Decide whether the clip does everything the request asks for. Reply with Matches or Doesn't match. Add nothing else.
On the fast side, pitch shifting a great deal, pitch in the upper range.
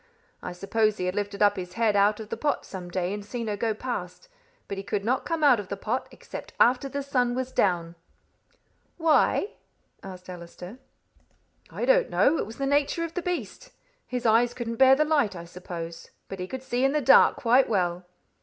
Matches